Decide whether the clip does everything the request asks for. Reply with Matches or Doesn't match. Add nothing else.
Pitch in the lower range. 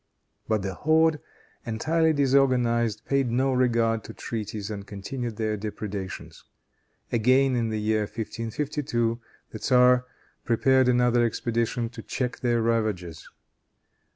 Matches